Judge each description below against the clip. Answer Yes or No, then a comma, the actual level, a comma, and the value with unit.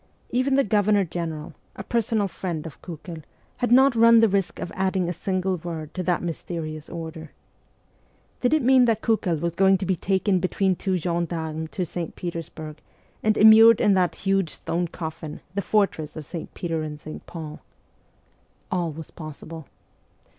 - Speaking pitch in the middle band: Yes, medium, 180 Hz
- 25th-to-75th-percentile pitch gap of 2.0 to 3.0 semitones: No, average, 3.9 semitones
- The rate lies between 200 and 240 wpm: No, average, 170 wpm